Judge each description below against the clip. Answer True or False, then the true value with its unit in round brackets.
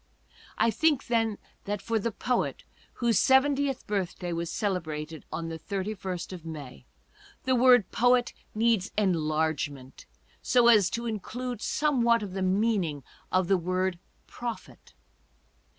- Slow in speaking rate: True (130 wpm)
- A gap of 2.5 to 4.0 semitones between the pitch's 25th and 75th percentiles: False (5.4 semitones)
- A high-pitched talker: True (200 Hz)